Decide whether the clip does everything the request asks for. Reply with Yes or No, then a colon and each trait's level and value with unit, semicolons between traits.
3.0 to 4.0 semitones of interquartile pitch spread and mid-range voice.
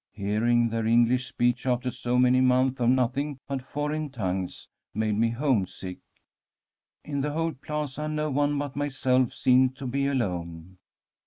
No: average, 3.3 semitones; low, 130 Hz